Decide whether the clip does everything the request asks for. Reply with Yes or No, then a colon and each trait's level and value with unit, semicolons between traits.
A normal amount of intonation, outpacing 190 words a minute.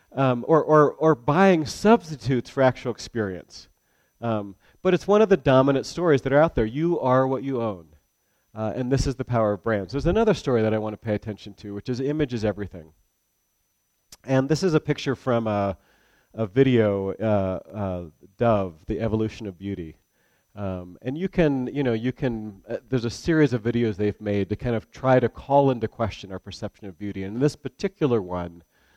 Yes: average, 5.0 semitones; fast, 205 wpm